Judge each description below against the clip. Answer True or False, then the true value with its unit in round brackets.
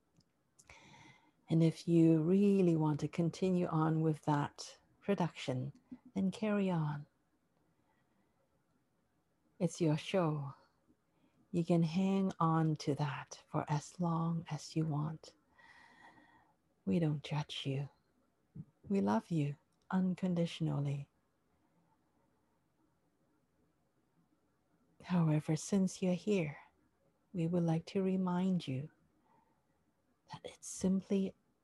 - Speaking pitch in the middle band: True (165 Hz)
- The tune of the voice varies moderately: True (3.7 semitones)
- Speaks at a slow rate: True (95 wpm)